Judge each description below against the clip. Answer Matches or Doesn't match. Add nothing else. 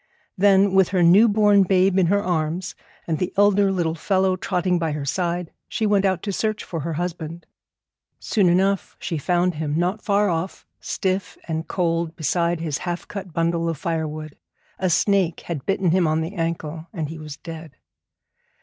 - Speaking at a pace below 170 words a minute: Doesn't match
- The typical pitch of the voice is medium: Matches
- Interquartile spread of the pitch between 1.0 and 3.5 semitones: Matches